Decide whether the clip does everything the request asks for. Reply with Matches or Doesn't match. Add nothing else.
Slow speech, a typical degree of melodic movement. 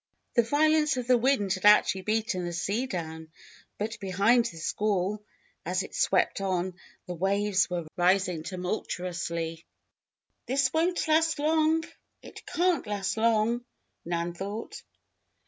Doesn't match